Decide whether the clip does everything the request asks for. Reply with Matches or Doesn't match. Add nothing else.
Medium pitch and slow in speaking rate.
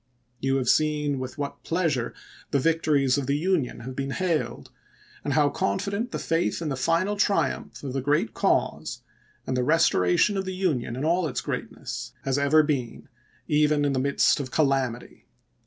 Doesn't match